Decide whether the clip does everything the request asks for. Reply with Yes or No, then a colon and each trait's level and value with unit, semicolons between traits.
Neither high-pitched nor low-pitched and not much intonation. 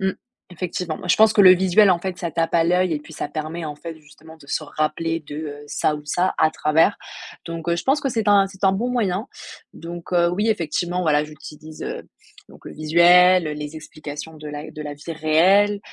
No: medium, 165 Hz; average, 3.2 semitones